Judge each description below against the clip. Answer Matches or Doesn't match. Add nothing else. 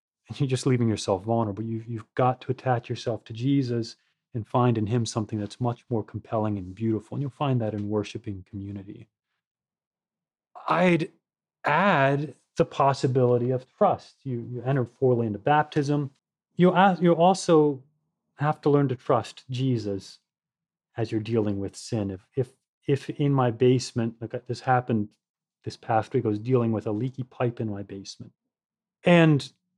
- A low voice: Matches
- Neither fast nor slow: Matches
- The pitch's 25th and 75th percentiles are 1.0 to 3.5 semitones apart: Doesn't match